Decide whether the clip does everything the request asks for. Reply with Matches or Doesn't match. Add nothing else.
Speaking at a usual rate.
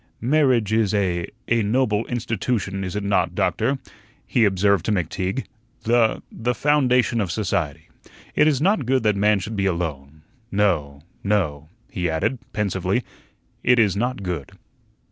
Matches